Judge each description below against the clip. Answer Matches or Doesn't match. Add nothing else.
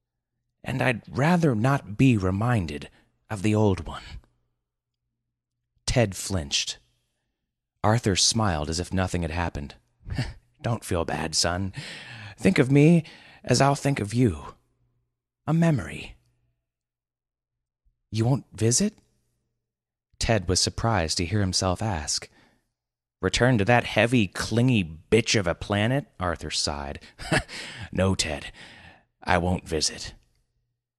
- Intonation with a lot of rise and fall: Matches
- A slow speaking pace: Matches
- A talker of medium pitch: Doesn't match